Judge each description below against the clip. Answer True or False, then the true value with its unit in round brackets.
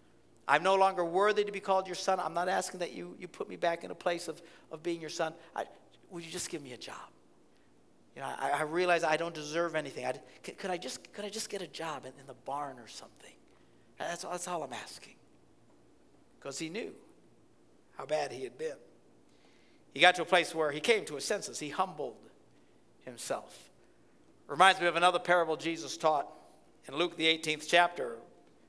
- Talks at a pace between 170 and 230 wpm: True (205 wpm)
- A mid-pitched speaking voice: True (170 Hz)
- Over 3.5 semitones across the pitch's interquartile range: False (3.1 semitones)